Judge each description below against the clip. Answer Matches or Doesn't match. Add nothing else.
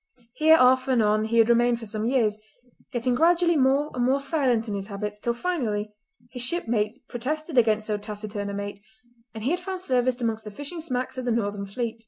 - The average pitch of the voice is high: Matches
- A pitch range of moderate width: Matches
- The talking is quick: Matches